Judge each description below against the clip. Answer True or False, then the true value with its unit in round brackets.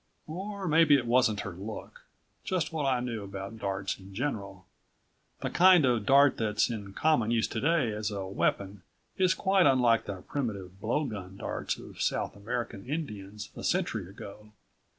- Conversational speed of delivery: True (160 wpm)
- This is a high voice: False (115 Hz)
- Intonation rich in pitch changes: True (6.4 semitones)